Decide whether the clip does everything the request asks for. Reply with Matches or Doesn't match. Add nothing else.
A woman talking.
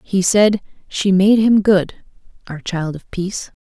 Matches